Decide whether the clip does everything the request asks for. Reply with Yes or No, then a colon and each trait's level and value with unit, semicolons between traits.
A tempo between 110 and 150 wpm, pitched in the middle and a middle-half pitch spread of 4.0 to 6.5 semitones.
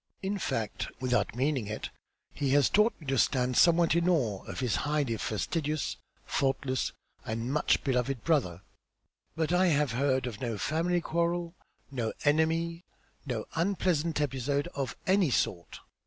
Yes: average, 145 wpm; medium, 145 Hz; average, 5.1 semitones